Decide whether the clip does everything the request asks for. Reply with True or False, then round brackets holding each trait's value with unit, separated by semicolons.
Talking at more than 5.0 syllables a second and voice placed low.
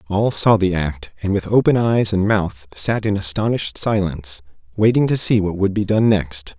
False (4.9 syllables/s; 100 Hz)